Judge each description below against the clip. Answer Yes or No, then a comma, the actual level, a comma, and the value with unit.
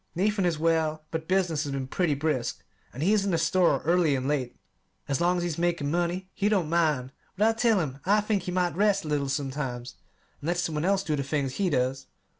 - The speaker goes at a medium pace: No, fast, 235 wpm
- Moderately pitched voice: Yes, medium, 165 Hz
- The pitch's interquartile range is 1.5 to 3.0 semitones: No, average, 4.4 semitones